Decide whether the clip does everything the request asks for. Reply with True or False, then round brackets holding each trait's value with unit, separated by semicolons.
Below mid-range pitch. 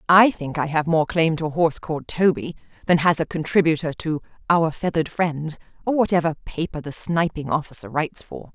False (160 Hz)